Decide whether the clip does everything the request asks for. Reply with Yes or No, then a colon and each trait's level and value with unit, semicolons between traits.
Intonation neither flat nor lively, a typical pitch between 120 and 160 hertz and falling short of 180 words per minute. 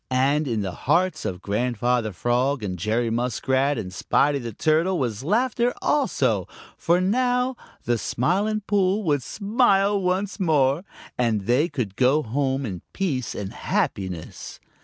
No: wide, 8.2 semitones; low, 135 Hz; average, 140 wpm